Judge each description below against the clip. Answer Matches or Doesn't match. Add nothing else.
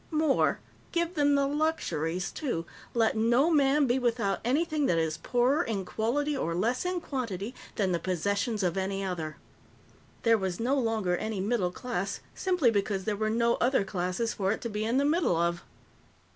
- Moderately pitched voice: Doesn't match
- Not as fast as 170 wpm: Doesn't match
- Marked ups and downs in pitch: Matches